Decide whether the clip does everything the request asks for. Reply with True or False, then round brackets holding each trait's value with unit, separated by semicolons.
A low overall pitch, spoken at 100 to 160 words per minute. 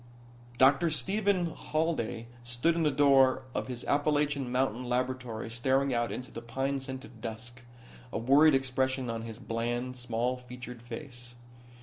True (130 Hz; 140 wpm)